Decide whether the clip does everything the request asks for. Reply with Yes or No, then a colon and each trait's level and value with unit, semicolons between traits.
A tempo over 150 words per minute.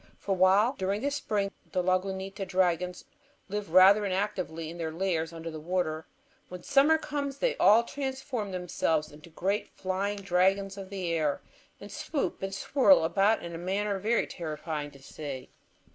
Yes: average, 160 wpm